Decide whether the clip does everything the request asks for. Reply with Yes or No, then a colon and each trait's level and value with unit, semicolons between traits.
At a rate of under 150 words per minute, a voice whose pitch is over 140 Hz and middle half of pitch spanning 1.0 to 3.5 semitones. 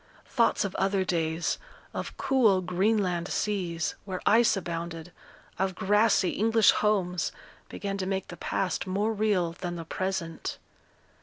Yes: slow, 135 wpm; high, 190 Hz; average, 2.9 semitones